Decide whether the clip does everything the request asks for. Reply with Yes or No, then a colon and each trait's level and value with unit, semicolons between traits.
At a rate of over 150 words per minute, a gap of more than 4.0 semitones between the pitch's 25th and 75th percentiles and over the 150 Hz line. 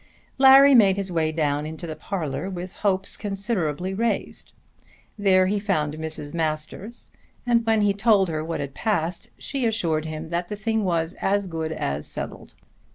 Yes: average, 165 wpm; average, 4.6 semitones; medium, 185 Hz